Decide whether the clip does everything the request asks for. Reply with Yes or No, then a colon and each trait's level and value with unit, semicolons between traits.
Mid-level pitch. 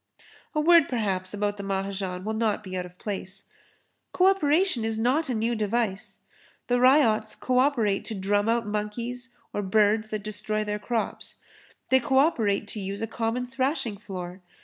No: high, 215 Hz